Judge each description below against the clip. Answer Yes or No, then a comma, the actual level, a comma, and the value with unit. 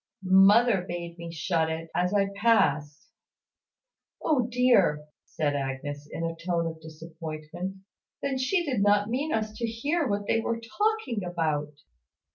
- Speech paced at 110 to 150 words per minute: Yes, average, 145 wpm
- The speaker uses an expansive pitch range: Yes, wide, 6.2 semitones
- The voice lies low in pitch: No, medium, 185 Hz